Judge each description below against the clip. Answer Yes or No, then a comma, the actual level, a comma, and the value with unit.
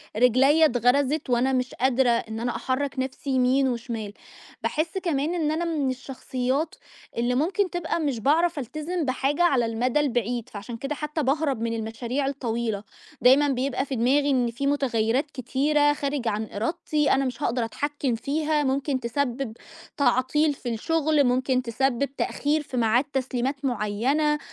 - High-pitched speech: Yes, very high, 265 Hz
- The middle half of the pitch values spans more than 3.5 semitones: No, average, 3.2 semitones